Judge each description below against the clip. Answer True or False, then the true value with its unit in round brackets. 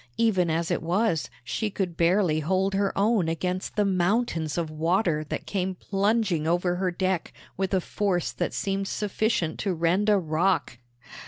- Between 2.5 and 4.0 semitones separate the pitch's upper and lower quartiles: True (3.0 semitones)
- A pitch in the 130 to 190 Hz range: True (185 Hz)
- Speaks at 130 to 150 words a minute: False (165 wpm)